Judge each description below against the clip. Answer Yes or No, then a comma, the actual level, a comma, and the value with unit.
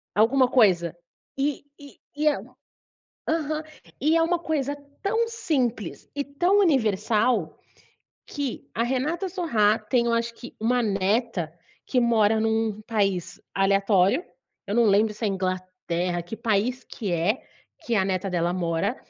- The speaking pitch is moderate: No, high, 225 Hz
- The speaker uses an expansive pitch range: Yes, wide, 5.9 semitones